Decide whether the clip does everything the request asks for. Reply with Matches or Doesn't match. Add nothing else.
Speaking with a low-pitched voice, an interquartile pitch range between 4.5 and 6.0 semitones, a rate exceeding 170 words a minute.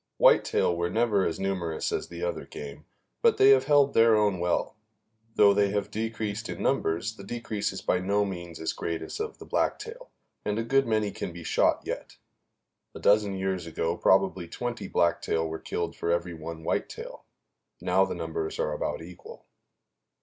Matches